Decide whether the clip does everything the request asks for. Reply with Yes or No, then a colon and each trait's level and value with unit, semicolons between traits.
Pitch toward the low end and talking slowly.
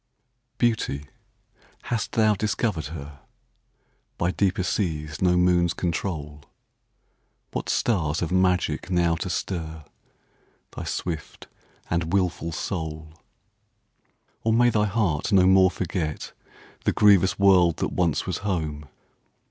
Yes: very low, 90 Hz; slow, 95 wpm